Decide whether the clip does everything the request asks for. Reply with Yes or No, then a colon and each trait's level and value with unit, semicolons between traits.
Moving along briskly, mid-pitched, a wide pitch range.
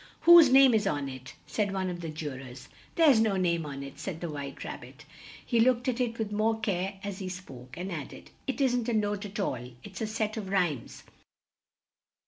No: fast, 220 wpm; high, 195 Hz; wide, 6.5 semitones